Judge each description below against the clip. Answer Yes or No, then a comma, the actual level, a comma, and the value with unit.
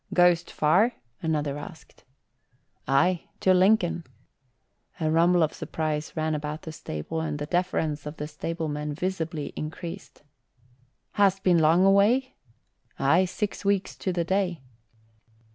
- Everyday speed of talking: No, slow, 125 wpm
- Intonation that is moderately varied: Yes, average, 3.4 semitones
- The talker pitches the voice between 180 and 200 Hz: No, medium, 165 Hz